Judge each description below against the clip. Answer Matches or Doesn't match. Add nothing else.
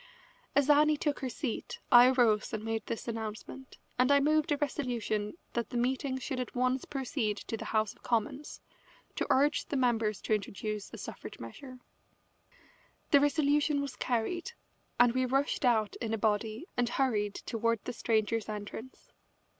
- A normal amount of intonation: Matches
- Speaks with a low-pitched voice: Doesn't match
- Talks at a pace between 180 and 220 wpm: Doesn't match